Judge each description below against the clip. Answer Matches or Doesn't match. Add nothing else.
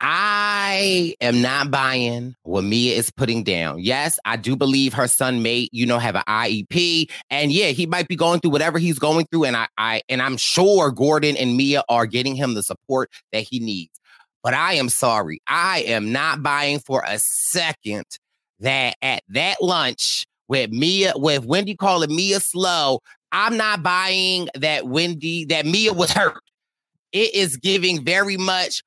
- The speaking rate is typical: Matches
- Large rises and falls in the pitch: Matches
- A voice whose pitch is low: Doesn't match